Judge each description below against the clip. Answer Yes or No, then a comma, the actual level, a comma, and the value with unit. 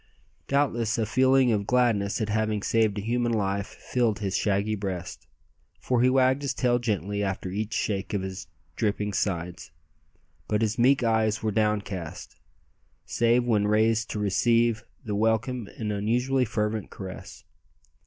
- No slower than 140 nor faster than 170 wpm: Yes, average, 150 wpm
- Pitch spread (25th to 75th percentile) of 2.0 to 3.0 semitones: Yes, average, 2.7 semitones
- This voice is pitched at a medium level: No, low, 110 Hz